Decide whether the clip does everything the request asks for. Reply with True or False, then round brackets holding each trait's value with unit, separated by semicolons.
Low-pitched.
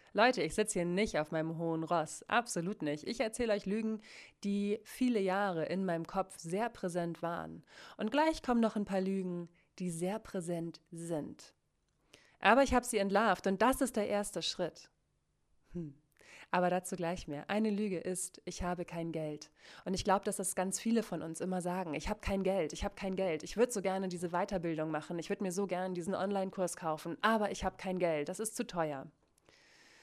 False (185 Hz)